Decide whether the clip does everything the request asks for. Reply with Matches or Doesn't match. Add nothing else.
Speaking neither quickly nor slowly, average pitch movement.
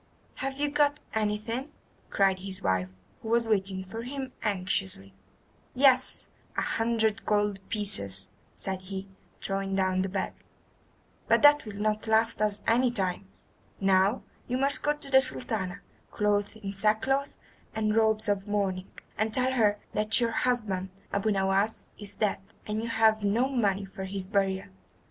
Matches